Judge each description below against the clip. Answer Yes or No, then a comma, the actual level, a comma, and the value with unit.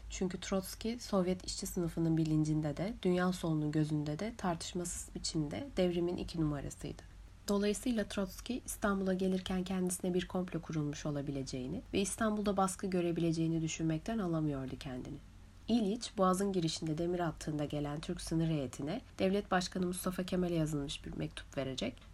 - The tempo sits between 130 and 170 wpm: Yes, average, 135 wpm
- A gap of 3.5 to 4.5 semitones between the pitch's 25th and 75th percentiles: Yes, average, 3.9 semitones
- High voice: No, medium, 175 Hz